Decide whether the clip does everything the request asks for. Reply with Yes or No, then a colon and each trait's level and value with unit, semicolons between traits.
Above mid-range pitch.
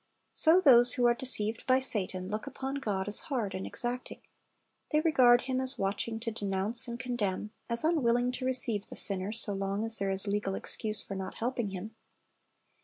Yes: high, 230 Hz